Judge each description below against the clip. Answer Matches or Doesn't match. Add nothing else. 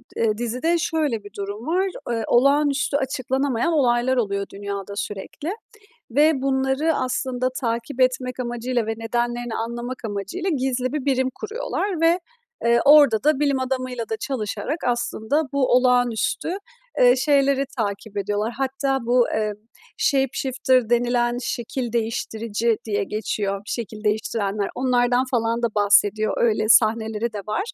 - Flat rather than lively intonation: Doesn't match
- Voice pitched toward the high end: Matches